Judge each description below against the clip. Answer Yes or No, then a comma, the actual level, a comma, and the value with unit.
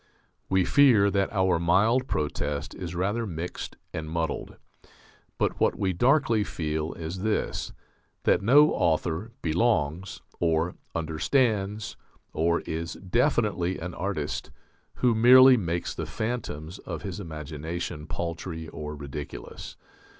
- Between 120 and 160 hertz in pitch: No, very low, 90 Hz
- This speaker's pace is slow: Yes, slow, 120 wpm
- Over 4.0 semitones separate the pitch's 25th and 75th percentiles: Yes, average, 5.0 semitones